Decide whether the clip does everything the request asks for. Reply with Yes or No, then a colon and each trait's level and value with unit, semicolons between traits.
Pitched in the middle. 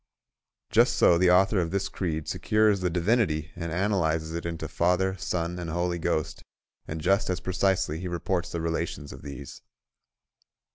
No: very low, 85 Hz